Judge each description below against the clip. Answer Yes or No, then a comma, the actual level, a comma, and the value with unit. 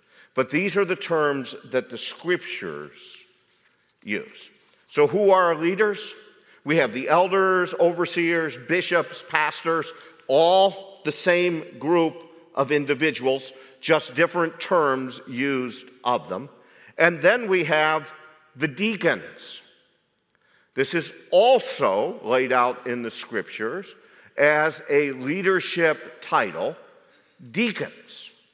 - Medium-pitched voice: Yes, medium, 165 Hz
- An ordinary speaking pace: No, slow, 110 wpm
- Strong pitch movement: No, average, 4.6 semitones